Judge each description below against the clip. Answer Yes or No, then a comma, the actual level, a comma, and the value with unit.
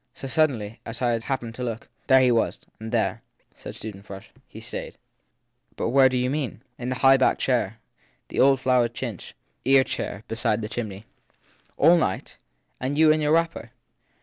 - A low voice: Yes, low, 125 Hz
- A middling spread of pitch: Yes, average, 3.1 semitones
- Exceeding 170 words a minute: Yes, average, 185 wpm